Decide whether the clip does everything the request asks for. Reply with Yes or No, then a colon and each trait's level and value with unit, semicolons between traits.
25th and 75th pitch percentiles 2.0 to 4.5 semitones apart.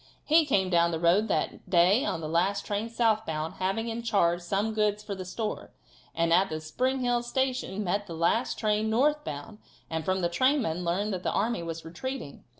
No: average, 5.1 semitones